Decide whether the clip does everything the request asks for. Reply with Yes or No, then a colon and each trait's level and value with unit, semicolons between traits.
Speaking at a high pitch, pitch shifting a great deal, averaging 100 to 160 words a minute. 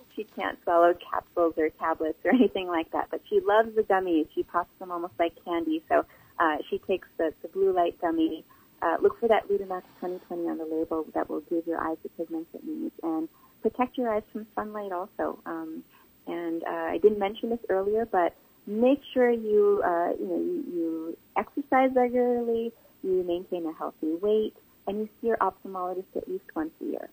No: high, 195 Hz; wide, 6.3 semitones; average, 195 wpm